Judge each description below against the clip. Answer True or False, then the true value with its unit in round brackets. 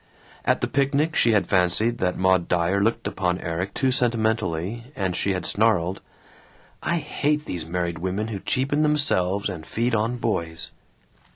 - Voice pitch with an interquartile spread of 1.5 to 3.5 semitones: False (4.8 semitones)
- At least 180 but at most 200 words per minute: False (160 wpm)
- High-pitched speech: False (100 Hz)